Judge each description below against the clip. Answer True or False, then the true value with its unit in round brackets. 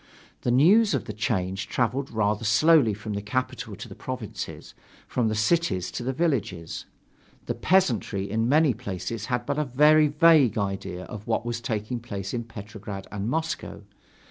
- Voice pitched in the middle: False (115 Hz)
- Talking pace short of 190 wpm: True (170 wpm)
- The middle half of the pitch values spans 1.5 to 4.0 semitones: False (5.2 semitones)